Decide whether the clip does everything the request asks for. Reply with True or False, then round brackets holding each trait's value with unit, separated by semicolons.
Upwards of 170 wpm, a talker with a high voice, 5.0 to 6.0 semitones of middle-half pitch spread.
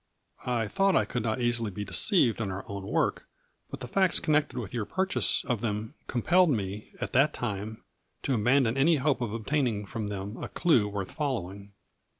False (195 wpm; 115 Hz; 5.3 semitones)